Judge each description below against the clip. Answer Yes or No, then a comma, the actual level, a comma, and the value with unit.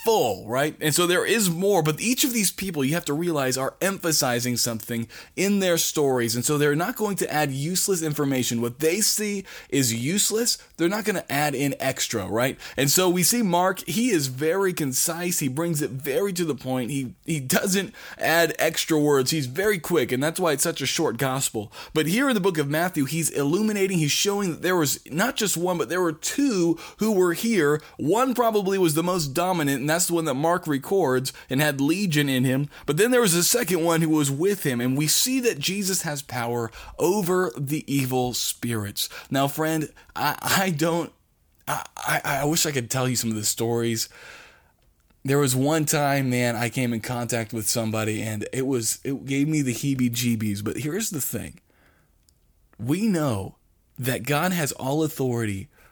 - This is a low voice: No, medium, 150 Hz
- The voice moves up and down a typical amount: No, wide, 5.7 semitones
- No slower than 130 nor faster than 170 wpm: No, average, 200 wpm